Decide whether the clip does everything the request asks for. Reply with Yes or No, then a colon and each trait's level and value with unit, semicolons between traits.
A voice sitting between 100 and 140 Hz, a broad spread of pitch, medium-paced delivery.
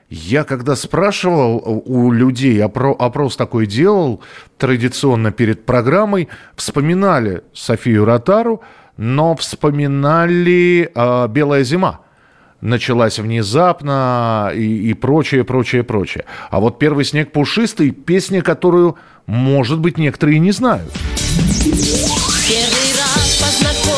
No: low, 135 Hz; wide, 6.0 semitones; slow, 100 wpm